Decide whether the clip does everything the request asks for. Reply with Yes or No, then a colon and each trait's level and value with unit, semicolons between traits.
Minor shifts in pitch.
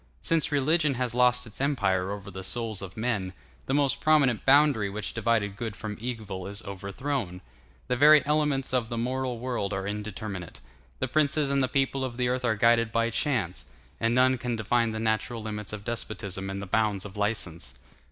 No: average, 4.1 semitones